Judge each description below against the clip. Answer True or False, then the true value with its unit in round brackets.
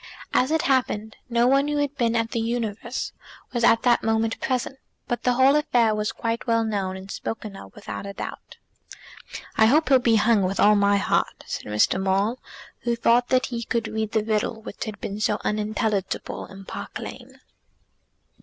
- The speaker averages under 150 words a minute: False (195 wpm)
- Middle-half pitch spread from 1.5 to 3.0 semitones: True (2.6 semitones)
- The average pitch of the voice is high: True (225 Hz)